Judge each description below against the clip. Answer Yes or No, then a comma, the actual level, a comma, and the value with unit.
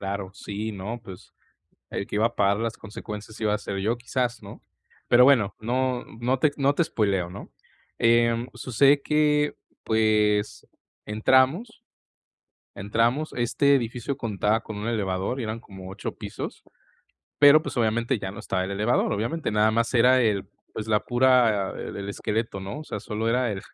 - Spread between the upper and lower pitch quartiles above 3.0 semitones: Yes, average, 3.5 semitones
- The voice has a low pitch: Yes, low, 115 Hz